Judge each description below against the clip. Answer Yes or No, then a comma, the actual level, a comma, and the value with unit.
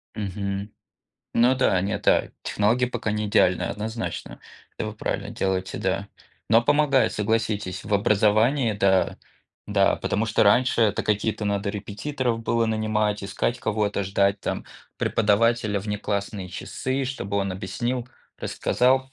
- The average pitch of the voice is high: No, low, 105 Hz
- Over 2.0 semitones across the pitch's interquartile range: Yes, narrow, 2.6 semitones